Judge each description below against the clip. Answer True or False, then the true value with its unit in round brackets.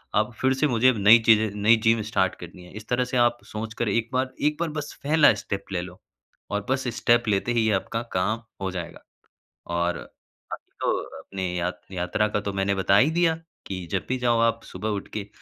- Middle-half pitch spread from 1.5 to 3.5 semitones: False (4.2 semitones)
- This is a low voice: True (110 Hz)